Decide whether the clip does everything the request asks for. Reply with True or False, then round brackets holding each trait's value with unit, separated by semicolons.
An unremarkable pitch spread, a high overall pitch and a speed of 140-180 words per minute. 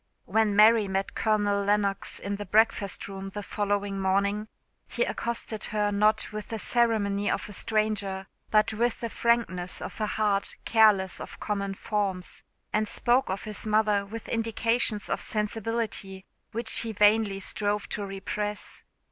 False (1.7 semitones; 210 Hz; 150 wpm)